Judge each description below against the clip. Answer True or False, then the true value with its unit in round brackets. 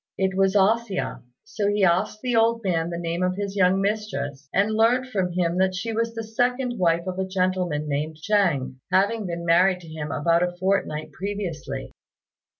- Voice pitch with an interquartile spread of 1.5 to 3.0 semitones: False (3.7 semitones)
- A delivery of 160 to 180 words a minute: False (190 wpm)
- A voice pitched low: False (190 Hz)